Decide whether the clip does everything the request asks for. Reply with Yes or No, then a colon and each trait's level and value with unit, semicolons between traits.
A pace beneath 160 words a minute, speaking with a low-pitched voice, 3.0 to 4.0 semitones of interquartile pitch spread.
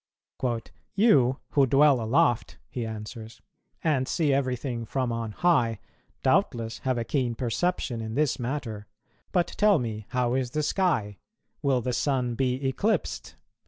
Yes: average, 140 wpm; low, 125 Hz; average, 3.6 semitones